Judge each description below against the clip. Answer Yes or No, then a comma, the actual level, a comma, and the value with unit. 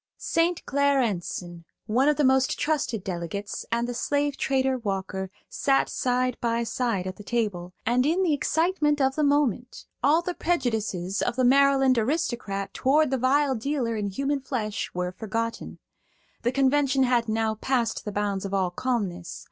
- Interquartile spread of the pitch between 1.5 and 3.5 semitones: No, average, 5.0 semitones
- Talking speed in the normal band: Yes, average, 165 wpm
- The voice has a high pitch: Yes, high, 245 Hz